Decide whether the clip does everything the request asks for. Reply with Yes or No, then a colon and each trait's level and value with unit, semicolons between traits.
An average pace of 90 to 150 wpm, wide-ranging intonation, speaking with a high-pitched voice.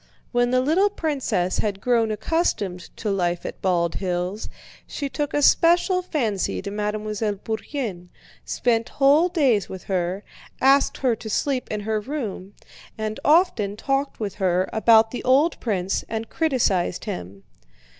Yes: average, 145 wpm; wide, 5.9 semitones; high, 220 Hz